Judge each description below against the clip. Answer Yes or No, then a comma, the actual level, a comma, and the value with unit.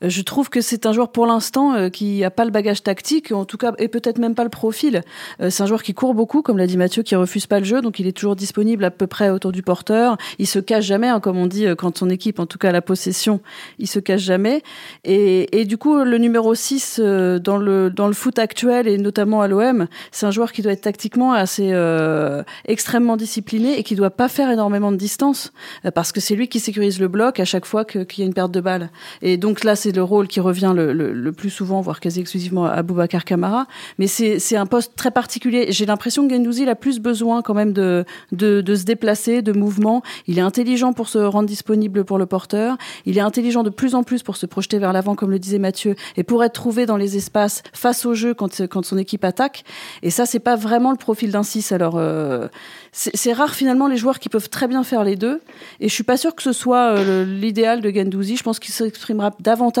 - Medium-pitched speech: No, high, 210 Hz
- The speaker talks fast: Yes, fast, 250 wpm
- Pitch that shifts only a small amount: No, average, 3.6 semitones